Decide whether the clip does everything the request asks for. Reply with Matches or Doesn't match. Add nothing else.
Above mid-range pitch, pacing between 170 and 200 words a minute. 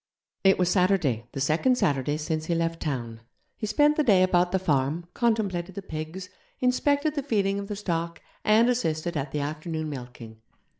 Doesn't match